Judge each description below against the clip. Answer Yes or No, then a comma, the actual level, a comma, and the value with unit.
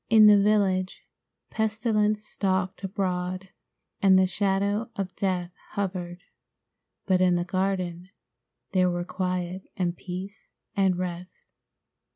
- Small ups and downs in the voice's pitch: Yes, narrow, 1.8 semitones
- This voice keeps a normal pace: No, slow, 115 wpm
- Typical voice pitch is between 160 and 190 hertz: Yes, medium, 185 Hz